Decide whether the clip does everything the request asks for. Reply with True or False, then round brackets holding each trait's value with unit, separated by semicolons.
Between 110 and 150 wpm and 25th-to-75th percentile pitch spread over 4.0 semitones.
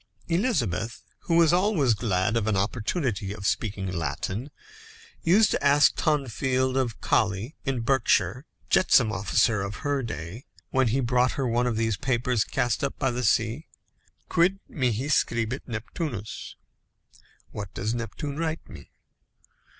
True (140 wpm; 4.5 semitones)